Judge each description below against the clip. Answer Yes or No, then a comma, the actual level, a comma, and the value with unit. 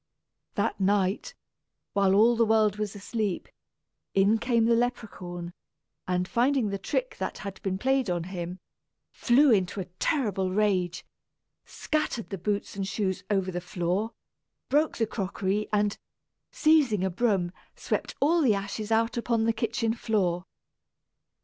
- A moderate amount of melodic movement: Yes, average, 3.5 semitones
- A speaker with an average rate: Yes, average, 145 wpm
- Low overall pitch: No, high, 210 Hz